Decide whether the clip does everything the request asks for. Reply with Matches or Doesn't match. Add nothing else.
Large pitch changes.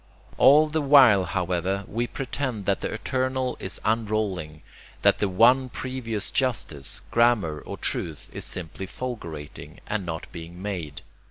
Matches